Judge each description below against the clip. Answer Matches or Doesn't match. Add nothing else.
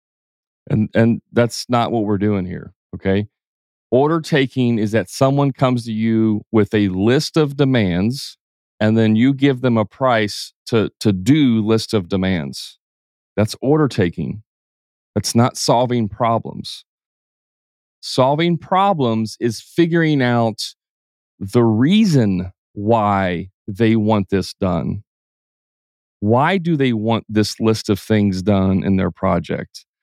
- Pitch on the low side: Matches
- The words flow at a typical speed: Doesn't match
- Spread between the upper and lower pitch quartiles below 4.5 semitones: Matches